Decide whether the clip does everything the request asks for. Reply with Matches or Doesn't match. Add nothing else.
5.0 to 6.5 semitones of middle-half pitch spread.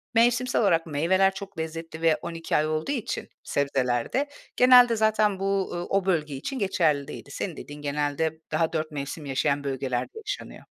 Matches